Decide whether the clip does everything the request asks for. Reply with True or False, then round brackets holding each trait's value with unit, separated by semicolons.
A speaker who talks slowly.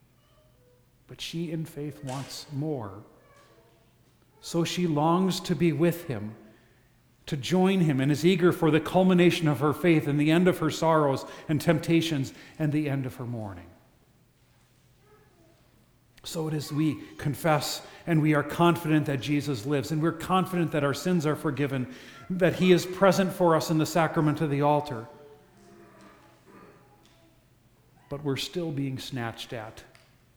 False (150 wpm)